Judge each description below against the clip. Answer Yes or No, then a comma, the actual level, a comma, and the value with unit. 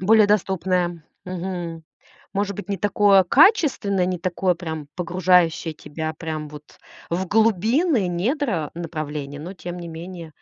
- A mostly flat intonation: No, average, 3.4 semitones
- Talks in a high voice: No, medium, 180 Hz